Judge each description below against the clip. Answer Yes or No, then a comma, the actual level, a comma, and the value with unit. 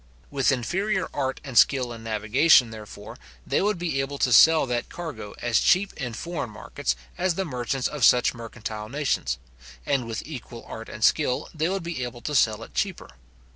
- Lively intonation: Yes, wide, 5.7 semitones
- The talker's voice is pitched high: No, low, 130 Hz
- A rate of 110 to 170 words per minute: No, average, 185 wpm